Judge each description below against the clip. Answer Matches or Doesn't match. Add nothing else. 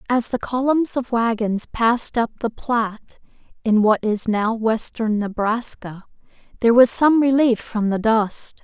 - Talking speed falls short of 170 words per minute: Matches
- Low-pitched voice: Doesn't match